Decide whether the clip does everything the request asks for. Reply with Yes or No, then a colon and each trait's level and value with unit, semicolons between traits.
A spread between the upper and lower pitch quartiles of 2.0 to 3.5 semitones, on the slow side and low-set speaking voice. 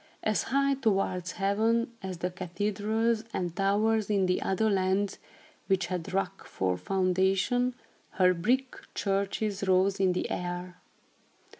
No: average, 2.8 semitones; slow, 125 wpm; high, 195 Hz